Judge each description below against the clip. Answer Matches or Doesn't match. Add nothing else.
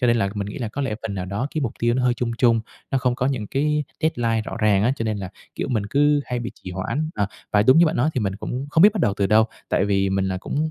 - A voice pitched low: Matches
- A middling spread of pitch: Matches